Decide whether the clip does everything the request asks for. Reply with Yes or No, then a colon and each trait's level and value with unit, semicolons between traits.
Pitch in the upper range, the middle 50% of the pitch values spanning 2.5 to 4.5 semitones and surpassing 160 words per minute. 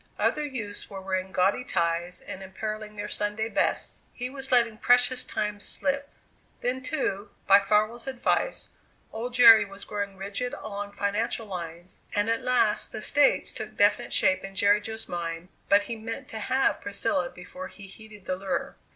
Yes: high, 210 Hz; average, 3.7 semitones; average, 170 wpm